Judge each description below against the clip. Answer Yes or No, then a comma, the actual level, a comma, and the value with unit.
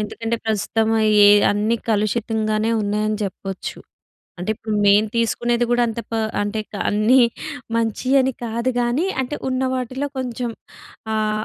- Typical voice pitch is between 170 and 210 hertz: No, high, 225 Hz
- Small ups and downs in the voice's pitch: Yes, narrow, 2.2 semitones